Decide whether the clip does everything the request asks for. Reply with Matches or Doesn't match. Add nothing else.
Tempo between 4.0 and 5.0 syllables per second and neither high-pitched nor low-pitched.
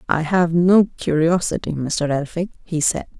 Matches